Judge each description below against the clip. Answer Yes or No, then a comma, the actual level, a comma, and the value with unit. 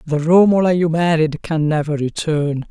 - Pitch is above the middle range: No, medium, 160 Hz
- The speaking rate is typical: Yes, average, 155 wpm